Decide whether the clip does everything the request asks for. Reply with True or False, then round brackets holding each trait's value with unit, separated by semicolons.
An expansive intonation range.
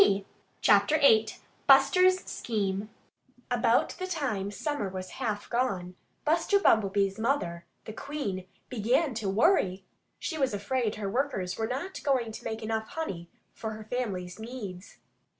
True (5.7 semitones)